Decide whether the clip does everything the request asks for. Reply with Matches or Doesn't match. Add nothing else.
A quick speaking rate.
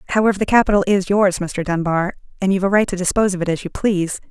Matches